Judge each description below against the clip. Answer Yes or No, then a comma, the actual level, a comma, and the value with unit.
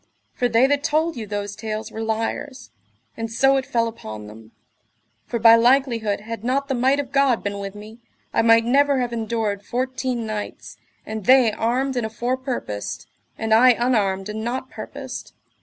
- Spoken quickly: No, average, 175 wpm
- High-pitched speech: Yes, high, 230 Hz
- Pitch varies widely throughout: No, average, 3.2 semitones